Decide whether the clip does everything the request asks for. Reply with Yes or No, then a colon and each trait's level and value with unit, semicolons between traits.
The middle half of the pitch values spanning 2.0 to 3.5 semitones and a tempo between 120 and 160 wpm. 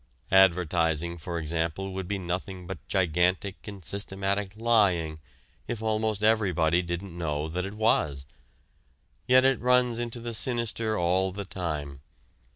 No: average, 4.0 semitones; slow, 135 wpm